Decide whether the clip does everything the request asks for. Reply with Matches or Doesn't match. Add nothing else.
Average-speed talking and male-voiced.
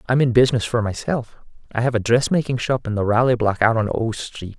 Doesn't match